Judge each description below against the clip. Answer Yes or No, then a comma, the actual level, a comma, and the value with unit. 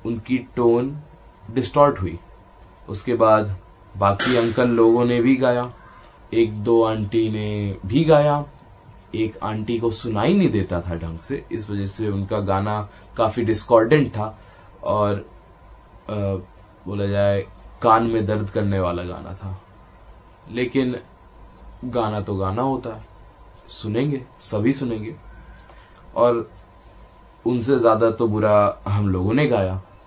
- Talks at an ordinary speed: Yes, average, 125 wpm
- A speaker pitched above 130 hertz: No, low, 110 Hz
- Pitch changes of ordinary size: Yes, average, 3.2 semitones